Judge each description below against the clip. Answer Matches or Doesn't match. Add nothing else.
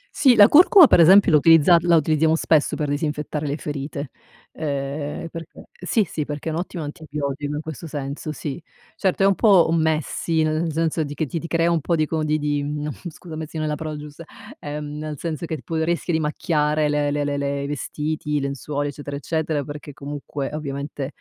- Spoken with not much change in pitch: Matches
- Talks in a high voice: Doesn't match